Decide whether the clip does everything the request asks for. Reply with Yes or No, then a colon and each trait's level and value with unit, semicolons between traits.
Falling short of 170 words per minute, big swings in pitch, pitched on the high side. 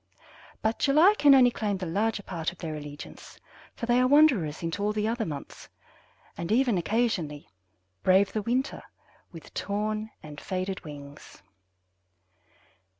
Yes: average, 145 wpm; wide, 6.2 semitones; high, 205 Hz